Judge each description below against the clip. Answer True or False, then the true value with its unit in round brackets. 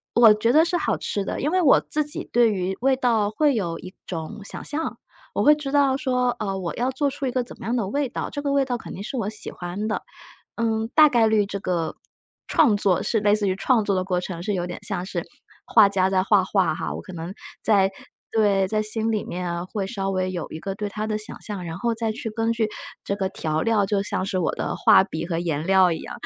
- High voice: True (210 Hz)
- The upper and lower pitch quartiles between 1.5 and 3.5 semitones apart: False (4.1 semitones)